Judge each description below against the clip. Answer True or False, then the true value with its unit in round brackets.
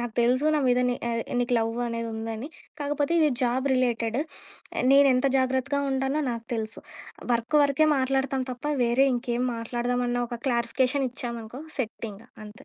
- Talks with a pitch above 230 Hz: True (245 Hz)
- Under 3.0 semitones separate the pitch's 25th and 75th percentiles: True (2.4 semitones)